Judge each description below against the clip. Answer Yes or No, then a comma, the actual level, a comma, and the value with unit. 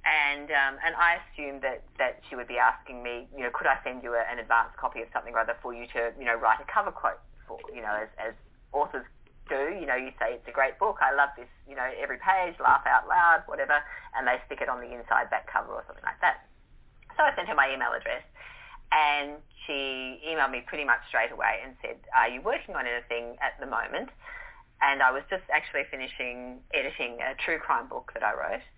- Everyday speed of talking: No, fast, 230 wpm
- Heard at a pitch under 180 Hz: Yes, low, 135 Hz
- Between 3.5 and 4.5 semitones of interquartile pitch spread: No, average, 5.1 semitones